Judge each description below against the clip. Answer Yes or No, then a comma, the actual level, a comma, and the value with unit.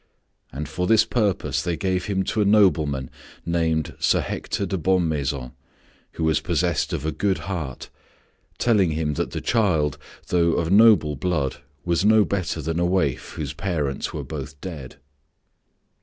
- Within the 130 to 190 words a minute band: Yes, average, 155 wpm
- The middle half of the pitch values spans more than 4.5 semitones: No, average, 4.0 semitones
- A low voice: Yes, very low, 85 Hz